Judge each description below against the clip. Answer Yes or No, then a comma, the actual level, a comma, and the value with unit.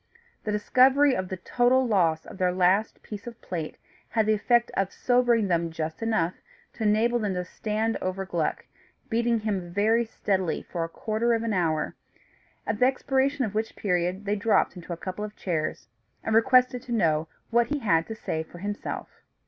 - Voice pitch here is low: No, high, 210 Hz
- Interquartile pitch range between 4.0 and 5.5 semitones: Yes, average, 4.6 semitones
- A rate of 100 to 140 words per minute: No, average, 190 wpm